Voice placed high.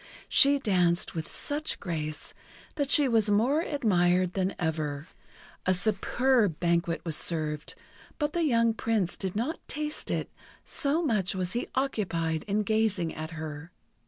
Yes: high, 195 Hz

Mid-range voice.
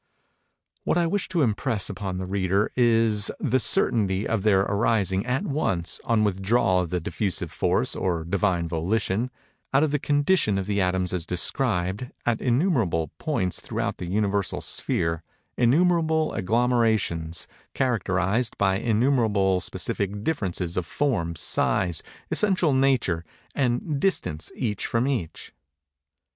No: low, 105 Hz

